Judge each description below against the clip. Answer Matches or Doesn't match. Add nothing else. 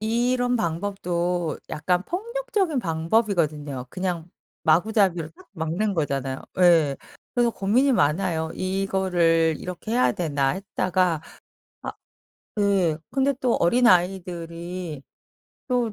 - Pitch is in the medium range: Matches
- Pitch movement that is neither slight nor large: Matches